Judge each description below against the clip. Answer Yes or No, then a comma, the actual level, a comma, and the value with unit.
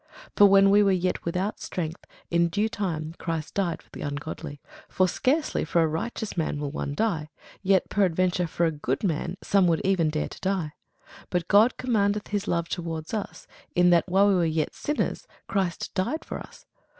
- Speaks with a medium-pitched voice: Yes, medium, 180 Hz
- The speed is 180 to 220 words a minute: Yes, average, 190 wpm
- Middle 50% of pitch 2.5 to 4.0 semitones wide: Yes, average, 3.5 semitones